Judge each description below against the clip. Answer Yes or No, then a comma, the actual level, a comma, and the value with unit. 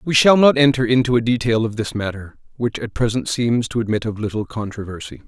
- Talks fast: Yes, fast, 215 wpm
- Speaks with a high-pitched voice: No, low, 115 Hz